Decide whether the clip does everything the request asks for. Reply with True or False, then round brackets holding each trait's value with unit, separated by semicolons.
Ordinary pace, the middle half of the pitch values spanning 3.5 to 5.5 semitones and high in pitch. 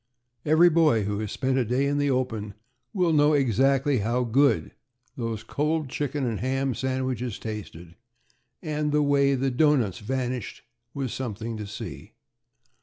False (150 wpm; 4.1 semitones; 130 Hz)